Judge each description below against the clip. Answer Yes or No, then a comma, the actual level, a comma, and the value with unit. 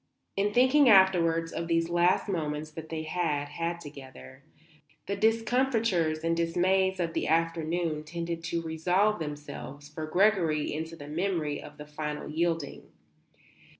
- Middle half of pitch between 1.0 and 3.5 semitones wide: Yes, average, 3.2 semitones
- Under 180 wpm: Yes, average, 140 wpm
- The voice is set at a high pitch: No, medium, 165 Hz